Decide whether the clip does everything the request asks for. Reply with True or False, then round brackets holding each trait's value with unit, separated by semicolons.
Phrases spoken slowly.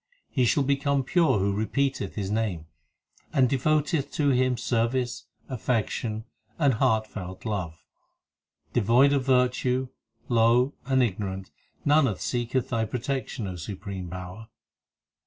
True (120 wpm)